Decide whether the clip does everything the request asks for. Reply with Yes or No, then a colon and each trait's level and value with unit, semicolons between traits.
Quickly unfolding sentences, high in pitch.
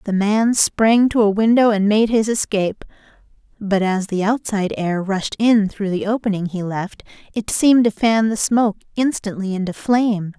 No: average, 180 wpm; high, 210 Hz